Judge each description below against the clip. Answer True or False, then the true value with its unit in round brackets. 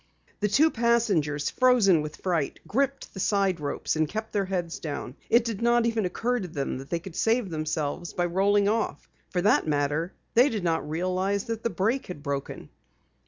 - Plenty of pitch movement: True (6.0 semitones)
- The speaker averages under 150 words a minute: False (190 wpm)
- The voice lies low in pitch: False (190 Hz)